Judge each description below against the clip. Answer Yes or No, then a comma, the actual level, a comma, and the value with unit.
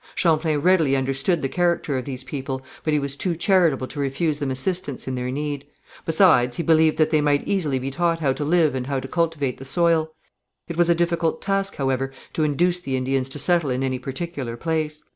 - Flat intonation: No, average, 4.0 semitones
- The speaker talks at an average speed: No, fast, 215 wpm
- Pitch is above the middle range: No, medium, 150 Hz